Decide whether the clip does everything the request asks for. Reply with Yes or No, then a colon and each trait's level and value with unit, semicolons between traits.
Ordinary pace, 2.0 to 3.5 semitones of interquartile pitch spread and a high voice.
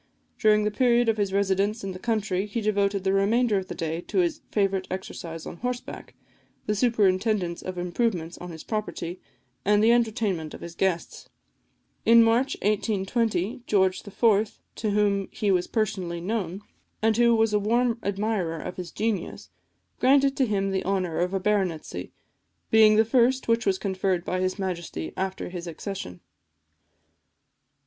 Yes: average, 160 wpm; average, 3.2 semitones; high, 200 Hz